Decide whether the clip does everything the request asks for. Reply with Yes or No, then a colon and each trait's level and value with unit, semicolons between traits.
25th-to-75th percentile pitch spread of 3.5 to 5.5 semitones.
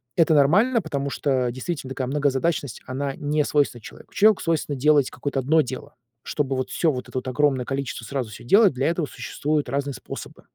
No: average, 2.9 semitones